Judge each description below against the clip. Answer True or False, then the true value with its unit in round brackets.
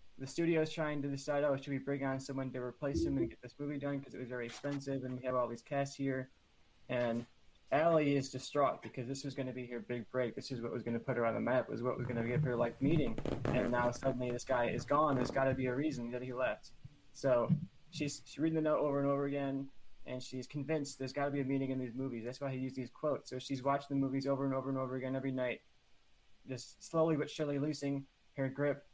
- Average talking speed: False (265 wpm)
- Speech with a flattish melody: True (2.1 semitones)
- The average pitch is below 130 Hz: False (135 Hz)